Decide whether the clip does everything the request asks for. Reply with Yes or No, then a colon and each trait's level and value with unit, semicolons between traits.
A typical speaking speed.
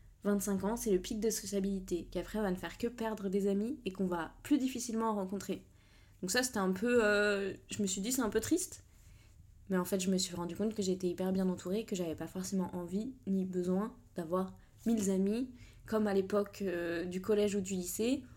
No: fast, 225 wpm